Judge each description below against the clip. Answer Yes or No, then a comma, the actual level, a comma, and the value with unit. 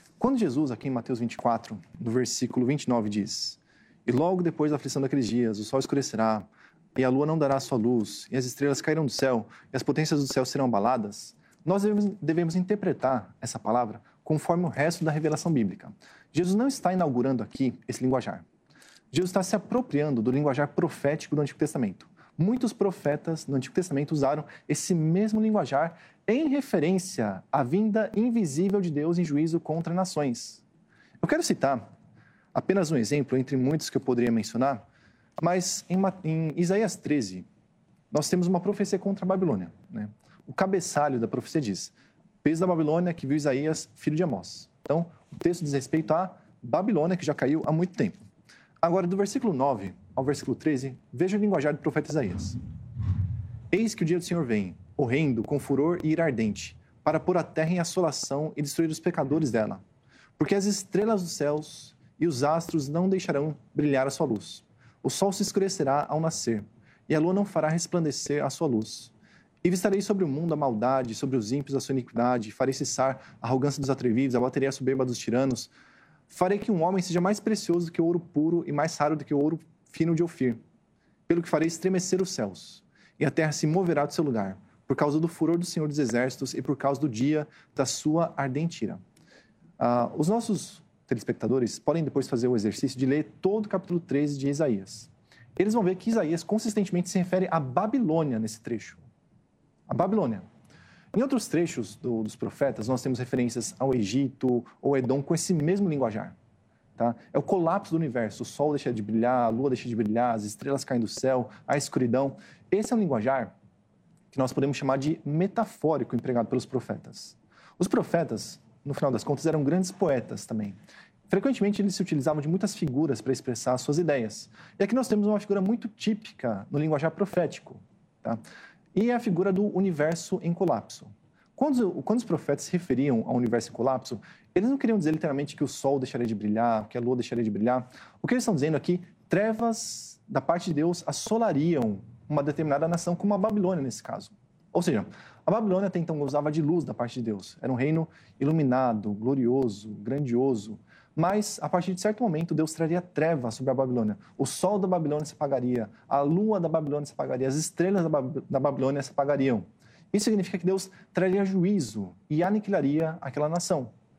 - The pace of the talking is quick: Yes, fast, 190 wpm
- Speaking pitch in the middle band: Yes, medium, 150 Hz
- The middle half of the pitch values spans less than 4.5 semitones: No, wide, 5.5 semitones